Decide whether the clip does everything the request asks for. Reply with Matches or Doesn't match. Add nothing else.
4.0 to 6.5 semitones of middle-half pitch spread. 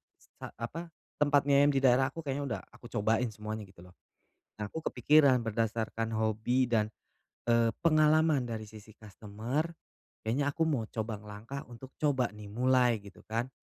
Matches